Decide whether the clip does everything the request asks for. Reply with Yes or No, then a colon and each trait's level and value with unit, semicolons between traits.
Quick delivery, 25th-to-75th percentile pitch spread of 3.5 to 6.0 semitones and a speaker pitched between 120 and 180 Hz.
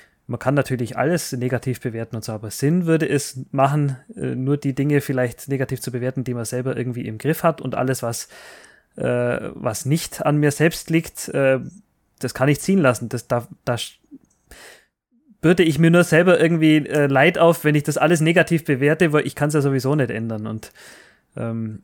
Yes: fast, 195 wpm; average, 4.2 semitones; medium, 140 Hz